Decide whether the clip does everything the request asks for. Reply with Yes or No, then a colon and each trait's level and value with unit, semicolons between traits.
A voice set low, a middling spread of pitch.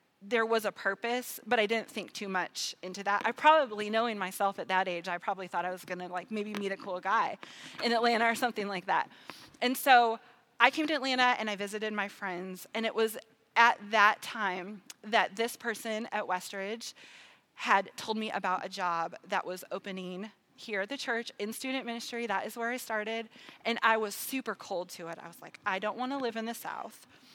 No: high, 215 Hz; average, 3.4 semitones